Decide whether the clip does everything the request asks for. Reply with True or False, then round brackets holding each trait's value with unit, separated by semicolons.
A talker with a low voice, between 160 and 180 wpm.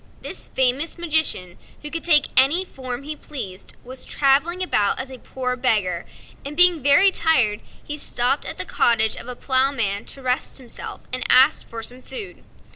False (265 Hz; 175 wpm)